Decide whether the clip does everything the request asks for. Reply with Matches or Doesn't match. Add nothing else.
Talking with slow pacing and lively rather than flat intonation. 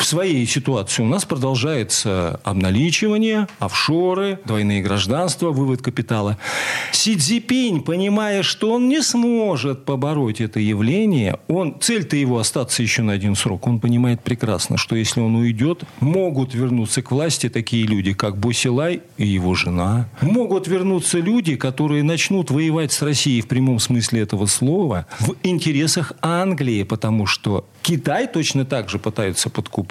Doesn't match